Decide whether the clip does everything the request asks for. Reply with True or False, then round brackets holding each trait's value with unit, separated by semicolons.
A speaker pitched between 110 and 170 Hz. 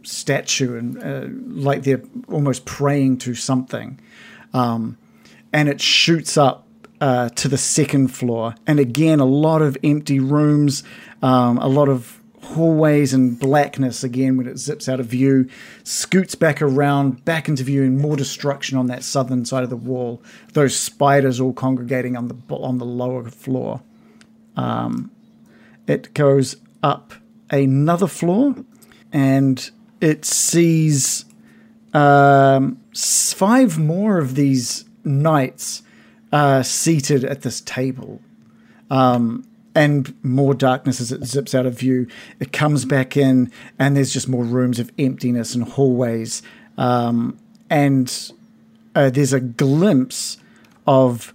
True (140 Hz)